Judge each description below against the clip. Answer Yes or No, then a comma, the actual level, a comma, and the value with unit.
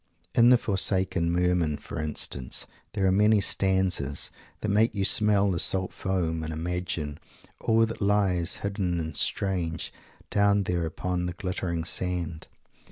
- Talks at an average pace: Yes, average, 145 wpm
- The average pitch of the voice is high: No, very low, 90 Hz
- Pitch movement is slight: No, average, 3.1 semitones